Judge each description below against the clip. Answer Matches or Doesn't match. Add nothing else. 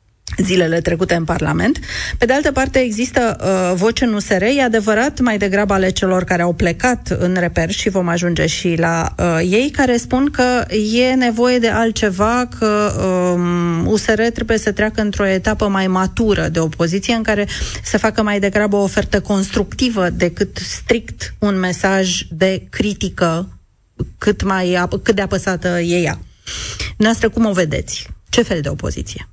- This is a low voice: Doesn't match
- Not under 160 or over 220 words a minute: Matches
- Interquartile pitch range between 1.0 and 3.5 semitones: Doesn't match